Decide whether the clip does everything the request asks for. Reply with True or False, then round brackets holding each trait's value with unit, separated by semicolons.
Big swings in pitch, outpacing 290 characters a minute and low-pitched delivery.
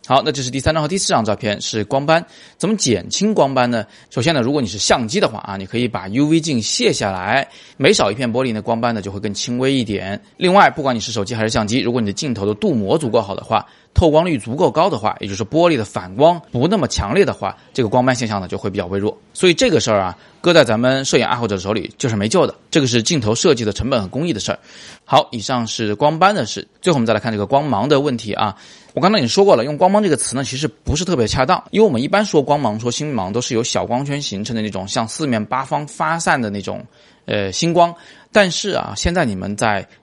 True (6.3 semitones; 380 characters per minute; 125 Hz)